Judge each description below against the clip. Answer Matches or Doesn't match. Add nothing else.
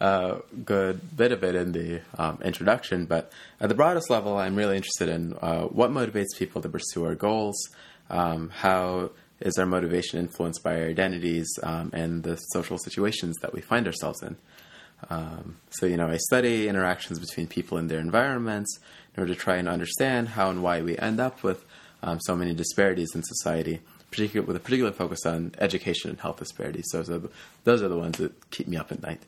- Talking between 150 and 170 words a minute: Doesn't match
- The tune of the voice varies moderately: Matches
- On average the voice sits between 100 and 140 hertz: Doesn't match